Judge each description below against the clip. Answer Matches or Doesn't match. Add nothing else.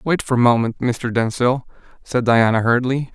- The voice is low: Matches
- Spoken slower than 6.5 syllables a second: Matches